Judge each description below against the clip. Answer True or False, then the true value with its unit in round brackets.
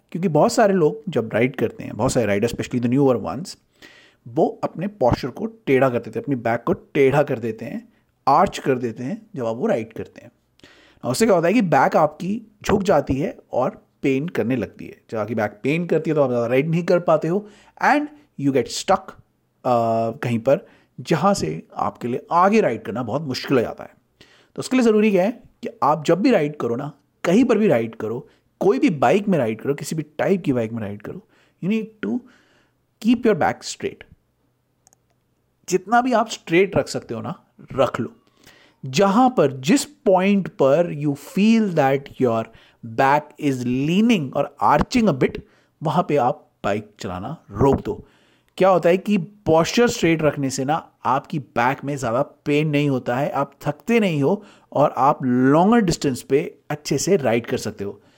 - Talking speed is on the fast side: True (195 wpm)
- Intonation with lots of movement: True (6.7 semitones)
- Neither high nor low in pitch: True (150 Hz)